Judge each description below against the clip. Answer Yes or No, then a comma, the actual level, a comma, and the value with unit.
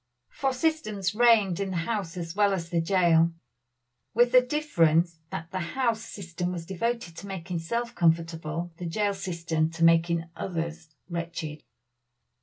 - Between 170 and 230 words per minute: No, average, 150 wpm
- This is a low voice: No, medium, 175 Hz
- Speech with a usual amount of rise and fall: Yes, average, 3.9 semitones